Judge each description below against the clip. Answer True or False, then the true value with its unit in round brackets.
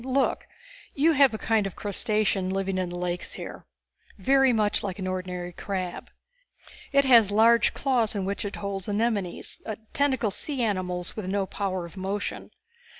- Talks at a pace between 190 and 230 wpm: False (160 wpm)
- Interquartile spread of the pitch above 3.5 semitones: True (3.9 semitones)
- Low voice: False (205 Hz)